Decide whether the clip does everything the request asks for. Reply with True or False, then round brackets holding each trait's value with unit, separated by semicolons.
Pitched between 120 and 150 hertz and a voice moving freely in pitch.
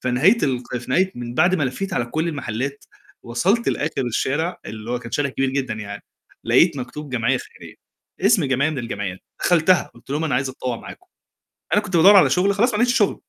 True (140 Hz; 6.6 semitones)